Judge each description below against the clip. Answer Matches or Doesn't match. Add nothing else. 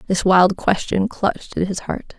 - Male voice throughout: Doesn't match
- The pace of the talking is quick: Doesn't match